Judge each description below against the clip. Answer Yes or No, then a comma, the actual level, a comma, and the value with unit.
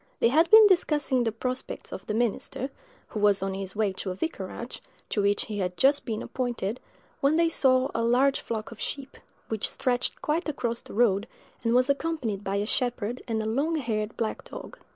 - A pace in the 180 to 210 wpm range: Yes, average, 200 wpm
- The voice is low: No, high, 235 Hz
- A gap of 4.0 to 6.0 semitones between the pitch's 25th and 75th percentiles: Yes, average, 4.4 semitones